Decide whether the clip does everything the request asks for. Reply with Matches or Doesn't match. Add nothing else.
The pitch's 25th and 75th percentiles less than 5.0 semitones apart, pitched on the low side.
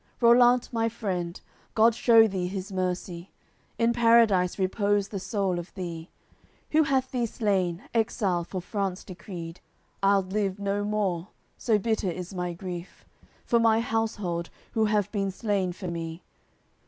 Doesn't match